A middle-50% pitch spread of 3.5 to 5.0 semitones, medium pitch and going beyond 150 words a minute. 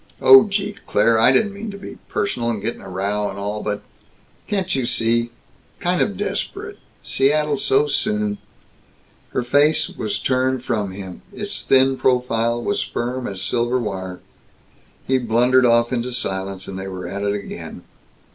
No: average, 4.4 semitones; low, 120 Hz; average, 170 wpm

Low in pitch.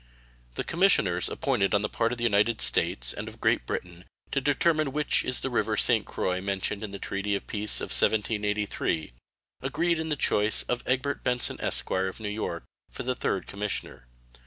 Yes: low, 105 Hz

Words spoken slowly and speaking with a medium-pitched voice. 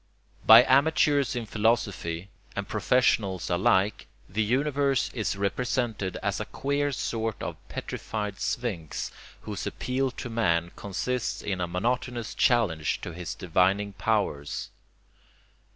No: slow, 120 wpm; low, 110 Hz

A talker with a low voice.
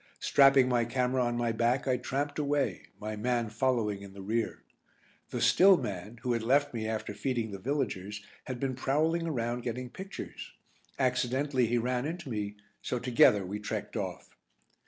Yes: low, 125 Hz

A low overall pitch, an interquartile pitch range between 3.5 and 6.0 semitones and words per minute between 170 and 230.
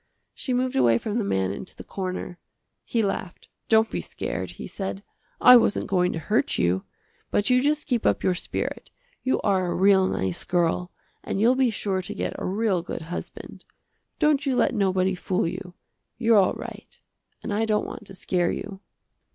No: high, 195 Hz; average, 4.0 semitones; average, 190 wpm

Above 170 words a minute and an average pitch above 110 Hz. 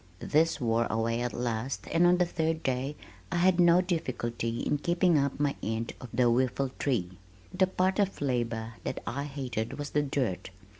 Yes: average, 180 wpm; low, 135 Hz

